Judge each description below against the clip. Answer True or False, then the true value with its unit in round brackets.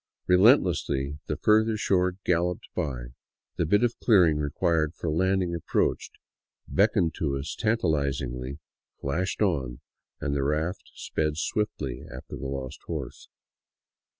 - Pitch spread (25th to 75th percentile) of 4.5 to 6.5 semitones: True (5.1 semitones)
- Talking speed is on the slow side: True (125 wpm)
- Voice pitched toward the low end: True (80 Hz)